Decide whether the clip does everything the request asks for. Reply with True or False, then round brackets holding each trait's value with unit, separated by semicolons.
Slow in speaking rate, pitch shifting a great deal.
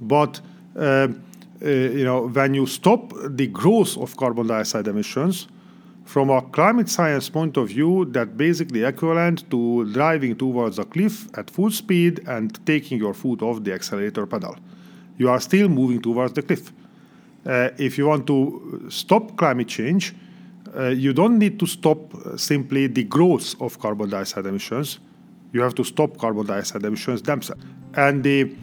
False (165 wpm; 6.4 semitones)